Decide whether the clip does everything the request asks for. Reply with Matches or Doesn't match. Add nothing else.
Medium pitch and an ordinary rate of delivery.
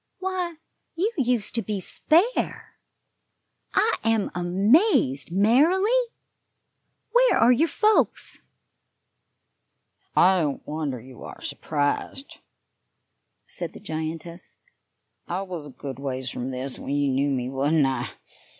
Doesn't match